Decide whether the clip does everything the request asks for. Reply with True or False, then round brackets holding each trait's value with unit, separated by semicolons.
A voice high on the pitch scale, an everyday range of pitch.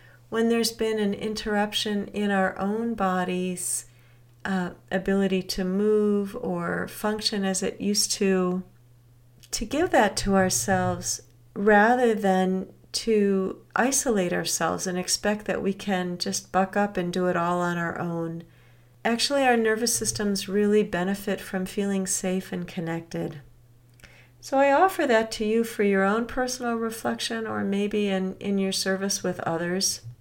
True (195 Hz; 3.3 semitones)